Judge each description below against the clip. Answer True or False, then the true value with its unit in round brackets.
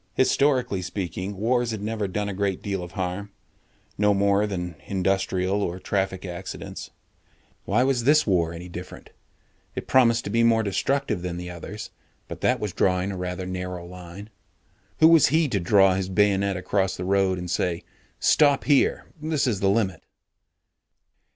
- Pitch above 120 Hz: False (100 Hz)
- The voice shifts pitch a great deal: False (3.2 semitones)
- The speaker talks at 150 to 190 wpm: True (170 wpm)